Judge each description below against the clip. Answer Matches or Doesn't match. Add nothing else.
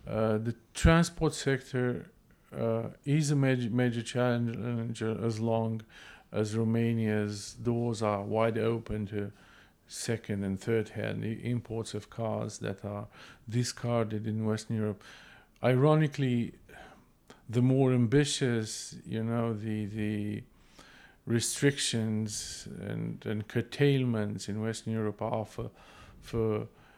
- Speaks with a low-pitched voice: Matches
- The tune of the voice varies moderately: Doesn't match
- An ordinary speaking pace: Doesn't match